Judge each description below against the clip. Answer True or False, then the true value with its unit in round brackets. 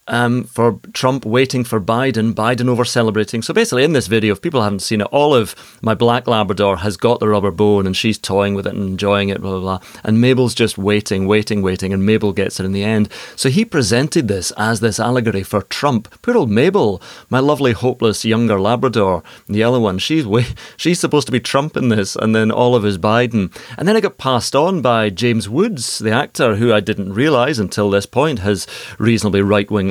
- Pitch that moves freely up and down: False (3.2 semitones)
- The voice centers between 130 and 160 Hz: False (110 Hz)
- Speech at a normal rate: False (215 wpm)